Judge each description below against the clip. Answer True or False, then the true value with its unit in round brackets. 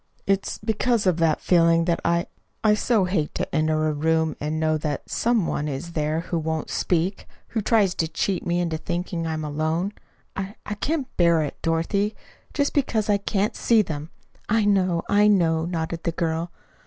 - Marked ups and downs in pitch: False (4.0 semitones)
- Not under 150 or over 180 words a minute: False (190 wpm)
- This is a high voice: False (170 Hz)